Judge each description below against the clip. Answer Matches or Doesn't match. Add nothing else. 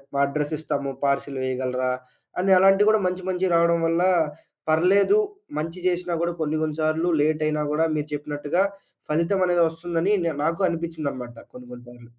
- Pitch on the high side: Doesn't match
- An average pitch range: Matches